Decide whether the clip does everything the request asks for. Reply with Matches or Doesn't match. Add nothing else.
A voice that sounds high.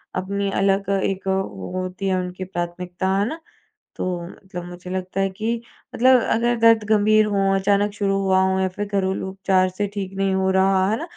Matches